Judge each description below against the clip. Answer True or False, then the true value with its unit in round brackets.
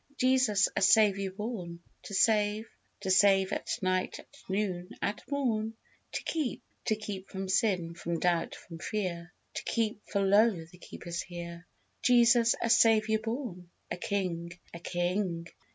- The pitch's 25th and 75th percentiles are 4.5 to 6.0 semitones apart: False (3.7 semitones)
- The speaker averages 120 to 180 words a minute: True (150 wpm)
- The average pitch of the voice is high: True (195 Hz)